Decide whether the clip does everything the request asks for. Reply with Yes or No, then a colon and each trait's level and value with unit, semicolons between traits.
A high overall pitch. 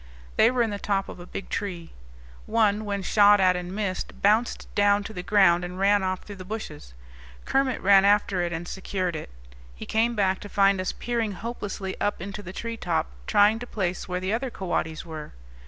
Yes: high, 200 Hz